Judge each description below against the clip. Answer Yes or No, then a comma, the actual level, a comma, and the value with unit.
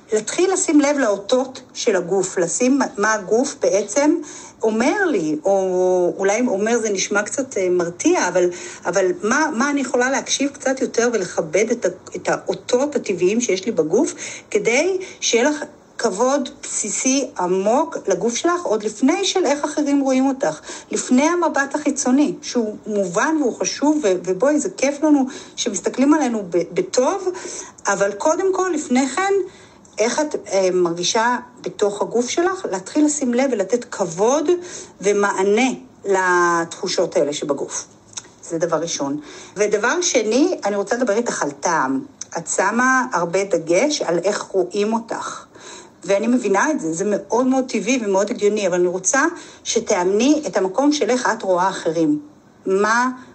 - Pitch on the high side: Yes, high, 240 Hz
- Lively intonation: Yes, wide, 6.8 semitones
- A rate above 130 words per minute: Yes, average, 140 wpm